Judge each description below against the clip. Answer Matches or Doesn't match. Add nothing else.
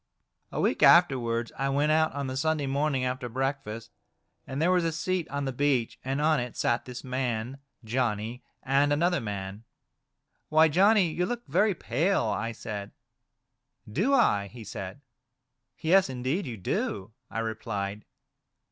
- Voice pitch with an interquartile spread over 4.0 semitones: Matches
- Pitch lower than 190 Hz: Matches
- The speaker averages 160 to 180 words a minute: Matches